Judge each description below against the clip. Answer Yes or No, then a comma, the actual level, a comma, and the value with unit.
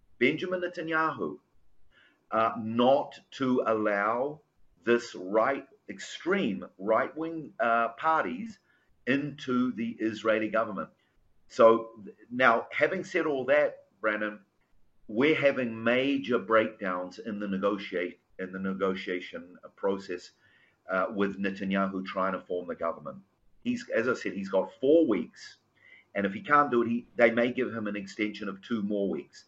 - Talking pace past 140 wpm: No, slow, 135 wpm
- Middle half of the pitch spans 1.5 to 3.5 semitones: No, wide, 5.4 semitones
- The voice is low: Yes, low, 115 Hz